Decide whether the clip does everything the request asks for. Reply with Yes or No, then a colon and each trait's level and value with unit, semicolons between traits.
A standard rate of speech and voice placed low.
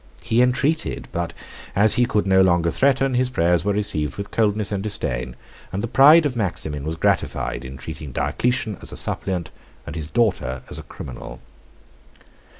Yes: average, 175 wpm; low, 100 Hz